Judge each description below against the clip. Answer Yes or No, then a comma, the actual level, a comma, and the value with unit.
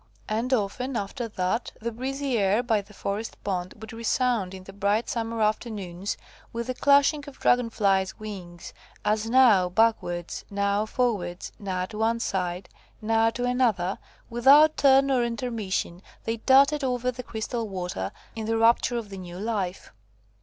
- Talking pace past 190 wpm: No, average, 160 wpm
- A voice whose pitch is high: Yes, high, 220 Hz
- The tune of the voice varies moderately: Yes, average, 3.9 semitones